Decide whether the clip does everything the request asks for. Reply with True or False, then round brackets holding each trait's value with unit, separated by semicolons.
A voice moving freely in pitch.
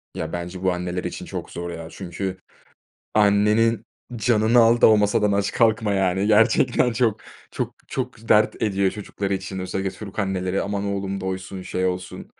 False (2.4 semitones)